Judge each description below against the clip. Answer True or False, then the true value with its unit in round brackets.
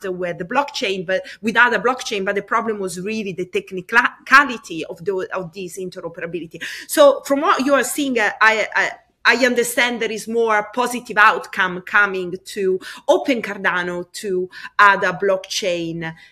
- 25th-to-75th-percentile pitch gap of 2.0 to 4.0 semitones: False (4.5 semitones)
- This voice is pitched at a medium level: False (210 Hz)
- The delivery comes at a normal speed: True (155 wpm)